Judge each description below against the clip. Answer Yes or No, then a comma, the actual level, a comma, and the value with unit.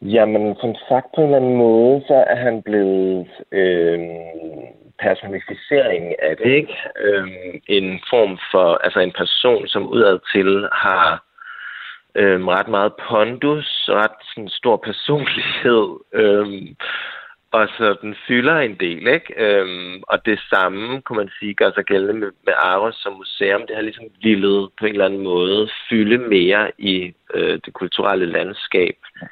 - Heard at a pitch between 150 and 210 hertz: No, low, 105 Hz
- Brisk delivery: No, average, 155 wpm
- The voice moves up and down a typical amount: Yes, average, 4.1 semitones